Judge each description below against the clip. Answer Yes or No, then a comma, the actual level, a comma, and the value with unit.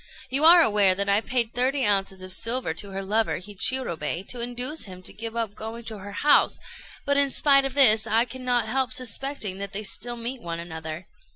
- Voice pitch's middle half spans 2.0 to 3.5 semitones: No, average, 4.6 semitones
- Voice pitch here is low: No, high, 225 Hz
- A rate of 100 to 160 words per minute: No, fast, 205 wpm